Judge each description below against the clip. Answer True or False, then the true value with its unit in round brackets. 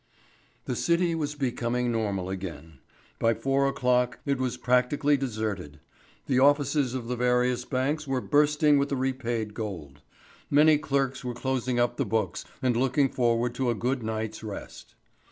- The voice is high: False (125 Hz)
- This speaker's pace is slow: False (155 wpm)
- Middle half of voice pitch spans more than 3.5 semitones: False (3.2 semitones)